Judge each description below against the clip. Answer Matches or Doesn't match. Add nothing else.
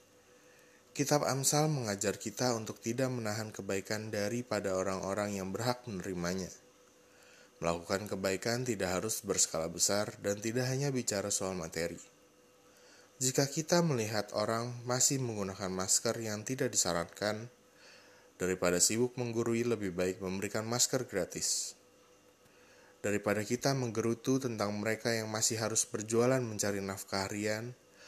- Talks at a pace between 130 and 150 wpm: Doesn't match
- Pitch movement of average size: Matches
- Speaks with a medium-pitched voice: Doesn't match